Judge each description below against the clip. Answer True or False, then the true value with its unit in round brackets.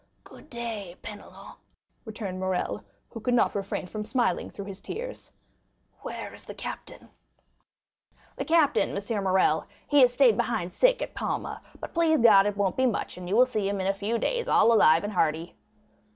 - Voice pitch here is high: True (210 Hz)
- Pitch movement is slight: False (4.1 semitones)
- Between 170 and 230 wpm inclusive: True (180 wpm)